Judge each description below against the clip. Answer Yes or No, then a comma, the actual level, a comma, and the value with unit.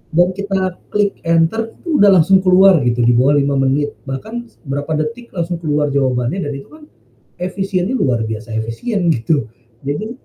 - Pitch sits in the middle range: Yes, medium, 165 Hz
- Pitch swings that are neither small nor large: No, wide, 6.2 semitones